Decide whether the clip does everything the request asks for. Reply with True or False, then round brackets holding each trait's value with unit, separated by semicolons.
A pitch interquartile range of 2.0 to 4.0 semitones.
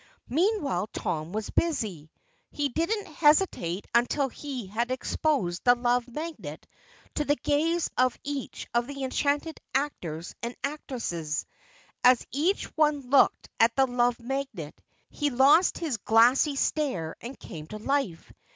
False (4.6 semitones)